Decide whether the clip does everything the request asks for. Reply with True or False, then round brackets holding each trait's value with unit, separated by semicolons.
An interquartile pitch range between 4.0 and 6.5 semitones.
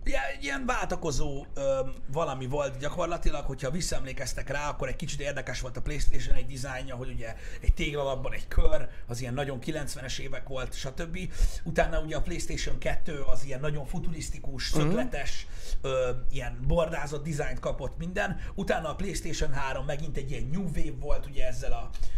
False (3.4 semitones)